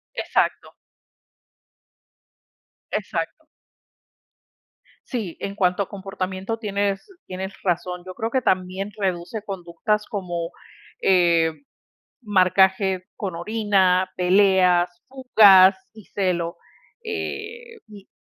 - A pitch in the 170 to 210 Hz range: Yes, high, 190 Hz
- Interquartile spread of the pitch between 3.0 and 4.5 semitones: No, narrow, 2.4 semitones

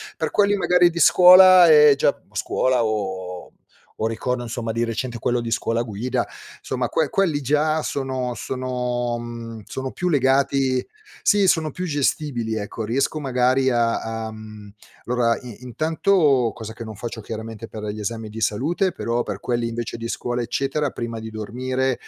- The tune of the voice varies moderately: Yes, average, 3.6 semitones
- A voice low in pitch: Yes, low, 120 Hz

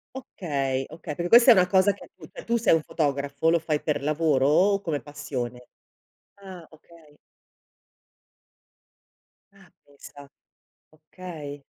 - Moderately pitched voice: Yes, medium, 155 Hz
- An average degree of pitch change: Yes, average, 4.2 semitones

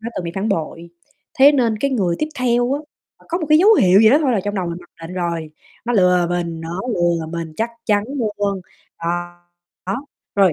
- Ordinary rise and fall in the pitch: No, wide, 5.9 semitones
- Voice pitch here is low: No, high, 195 Hz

